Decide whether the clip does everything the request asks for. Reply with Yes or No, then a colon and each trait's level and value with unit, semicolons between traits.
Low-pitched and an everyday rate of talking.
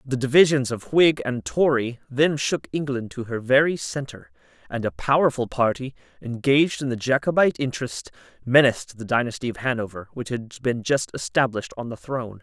Yes: low, 125 Hz; average, 170 wpm